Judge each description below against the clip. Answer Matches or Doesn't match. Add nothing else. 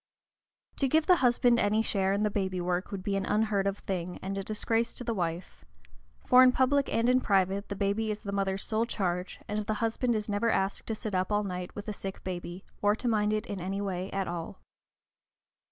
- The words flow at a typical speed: Doesn't match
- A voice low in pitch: Doesn't match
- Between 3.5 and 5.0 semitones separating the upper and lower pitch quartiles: Doesn't match